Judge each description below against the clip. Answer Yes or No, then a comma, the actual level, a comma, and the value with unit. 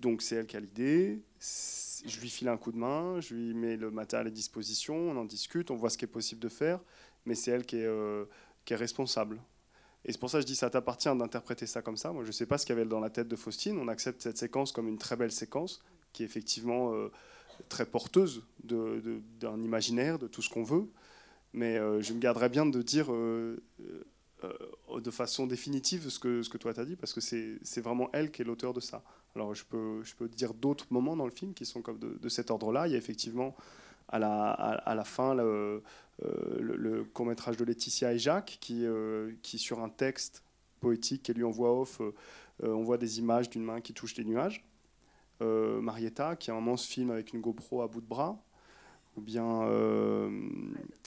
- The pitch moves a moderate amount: No, narrow, 1.9 semitones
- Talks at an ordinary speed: No, fast, 230 wpm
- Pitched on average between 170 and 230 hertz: No, low, 120 Hz